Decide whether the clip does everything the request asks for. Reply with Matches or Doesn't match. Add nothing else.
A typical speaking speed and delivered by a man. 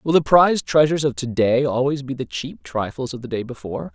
Doesn't match